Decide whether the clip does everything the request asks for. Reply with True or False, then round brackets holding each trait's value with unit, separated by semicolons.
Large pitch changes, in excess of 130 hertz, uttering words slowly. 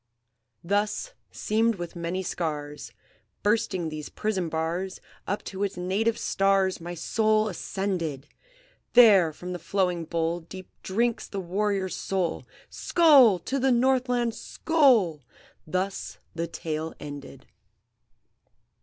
False (4.3 semitones; 190 Hz; 115 wpm)